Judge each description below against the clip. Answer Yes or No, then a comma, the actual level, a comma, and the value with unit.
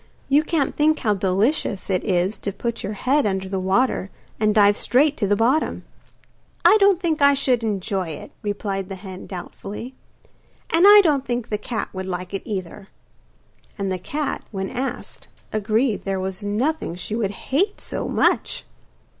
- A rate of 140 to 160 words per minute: No, average, 170 wpm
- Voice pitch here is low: No, high, 210 Hz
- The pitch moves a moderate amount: No, wide, 6.0 semitones